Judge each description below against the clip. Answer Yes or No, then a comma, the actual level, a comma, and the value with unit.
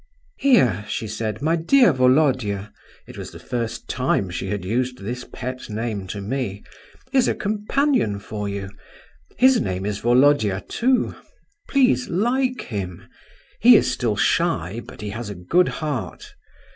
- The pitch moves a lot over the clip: Yes, wide, 8.3 semitones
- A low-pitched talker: Yes, low, 120 Hz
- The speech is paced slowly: No, average, 145 wpm